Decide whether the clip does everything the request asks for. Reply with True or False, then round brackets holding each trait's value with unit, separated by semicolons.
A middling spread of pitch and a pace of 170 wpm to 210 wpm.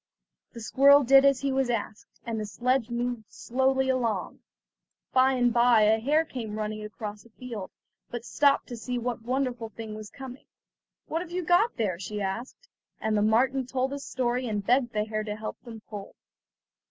True (3.5 semitones; 190 wpm)